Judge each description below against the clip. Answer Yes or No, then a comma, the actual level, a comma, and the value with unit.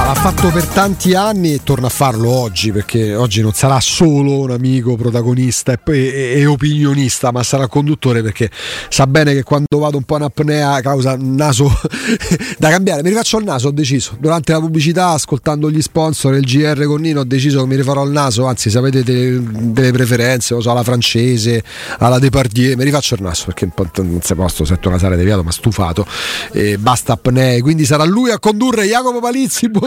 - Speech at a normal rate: No, fast, 190 wpm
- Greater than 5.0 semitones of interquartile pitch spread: No, average, 4.1 semitones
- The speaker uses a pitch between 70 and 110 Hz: No, low, 135 Hz